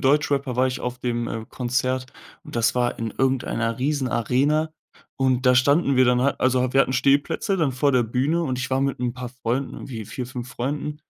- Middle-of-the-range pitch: No, low, 130 Hz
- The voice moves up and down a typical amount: No, narrow, 1.9 semitones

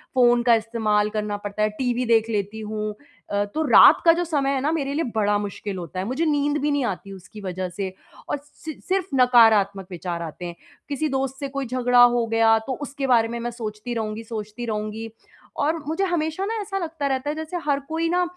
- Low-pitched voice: No, high, 235 Hz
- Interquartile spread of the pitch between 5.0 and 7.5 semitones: Yes, wide, 5.4 semitones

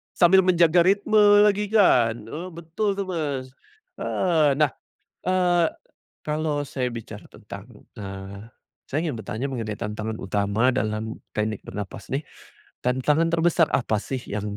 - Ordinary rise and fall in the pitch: No, wide, 7.7 semitones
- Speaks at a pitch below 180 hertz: Yes, low, 135 Hz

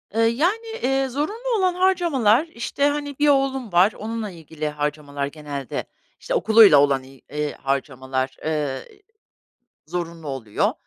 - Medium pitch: Yes, medium, 180 Hz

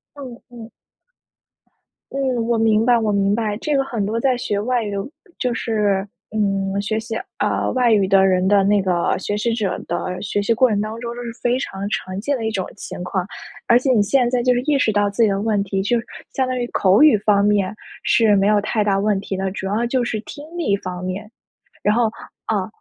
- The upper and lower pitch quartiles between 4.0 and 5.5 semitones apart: No, average, 3.1 semitones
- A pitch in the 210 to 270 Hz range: Yes, high, 215 Hz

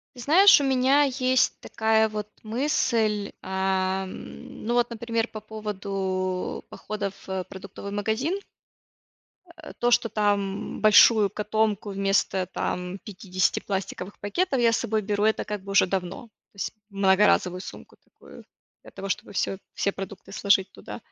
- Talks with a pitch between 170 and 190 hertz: No, high, 205 Hz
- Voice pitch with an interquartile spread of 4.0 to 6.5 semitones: No, average, 2.8 semitones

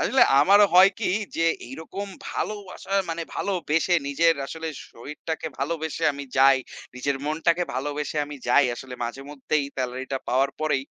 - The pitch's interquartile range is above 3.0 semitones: Yes, average, 3.6 semitones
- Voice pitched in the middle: Yes, medium, 150 Hz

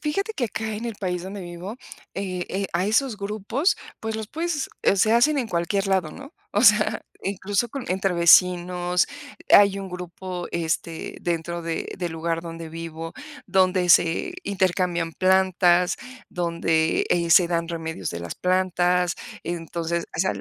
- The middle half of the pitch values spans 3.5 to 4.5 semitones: No, average, 2.9 semitones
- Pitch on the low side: No, medium, 180 Hz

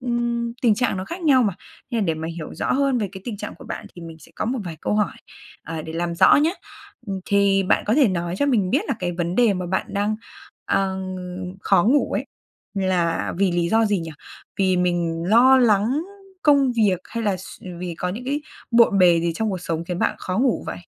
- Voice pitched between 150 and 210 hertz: Yes, high, 195 Hz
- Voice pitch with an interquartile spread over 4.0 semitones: Yes, average, 5.2 semitones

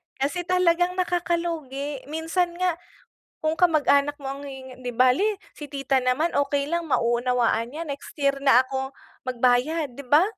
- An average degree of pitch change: Yes, average, 4.4 semitones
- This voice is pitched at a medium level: No, very high, 285 Hz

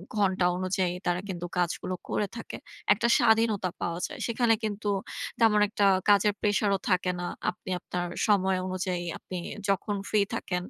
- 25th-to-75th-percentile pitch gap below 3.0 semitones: Yes, narrow, 2.6 semitones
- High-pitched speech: Yes, high, 195 Hz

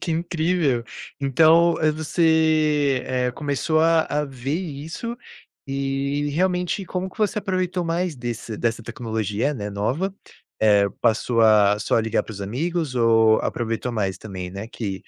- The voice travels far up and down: Yes, wide, 6.5 semitones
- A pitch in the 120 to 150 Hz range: Yes, medium, 140 Hz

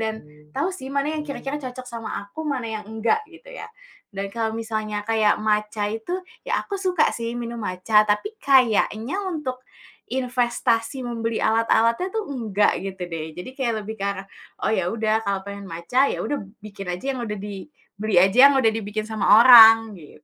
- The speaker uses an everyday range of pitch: Yes, average, 3.7 semitones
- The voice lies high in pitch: Yes, high, 225 Hz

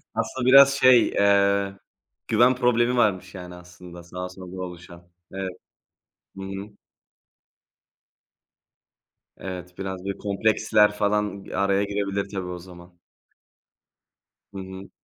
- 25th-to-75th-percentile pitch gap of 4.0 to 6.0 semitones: No, narrow, 2.4 semitones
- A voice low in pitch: Yes, low, 100 Hz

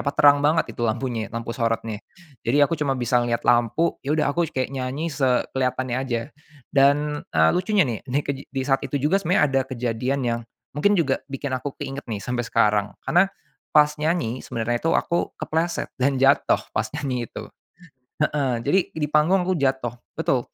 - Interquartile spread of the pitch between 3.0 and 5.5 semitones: Yes, average, 3.7 semitones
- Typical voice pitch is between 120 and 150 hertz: Yes, low, 135 Hz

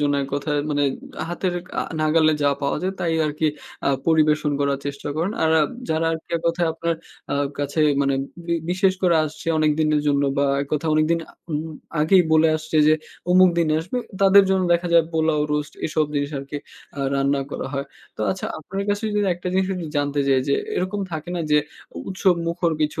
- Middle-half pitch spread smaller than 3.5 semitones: Yes, average, 2.9 semitones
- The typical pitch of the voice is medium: Yes, medium, 160 Hz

